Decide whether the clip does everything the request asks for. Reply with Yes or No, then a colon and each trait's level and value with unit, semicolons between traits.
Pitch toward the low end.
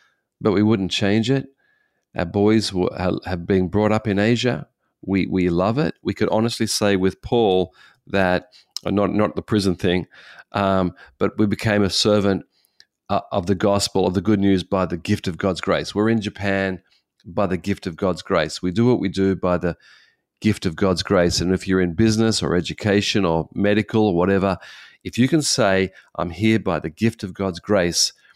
Yes: low, 100 Hz